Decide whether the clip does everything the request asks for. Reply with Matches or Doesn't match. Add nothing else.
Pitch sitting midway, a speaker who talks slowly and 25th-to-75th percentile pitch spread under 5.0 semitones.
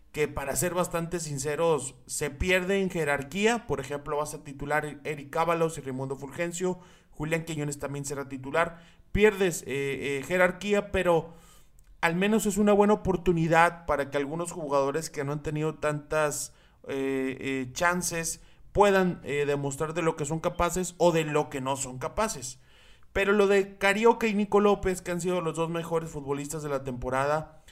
Doesn't match